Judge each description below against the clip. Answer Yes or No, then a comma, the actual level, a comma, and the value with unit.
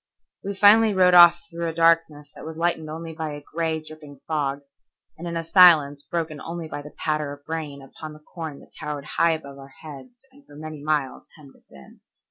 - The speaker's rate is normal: No, fast, 210 wpm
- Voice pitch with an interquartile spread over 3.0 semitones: No, narrow, 2.4 semitones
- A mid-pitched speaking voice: Yes, medium, 155 Hz